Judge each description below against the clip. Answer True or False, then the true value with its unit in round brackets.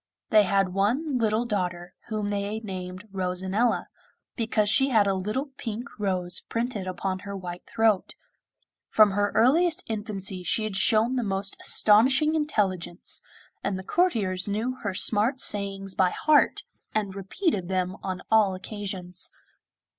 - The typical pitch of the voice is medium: False (205 Hz)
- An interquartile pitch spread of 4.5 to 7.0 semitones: False (3.1 semitones)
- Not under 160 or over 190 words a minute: False (145 wpm)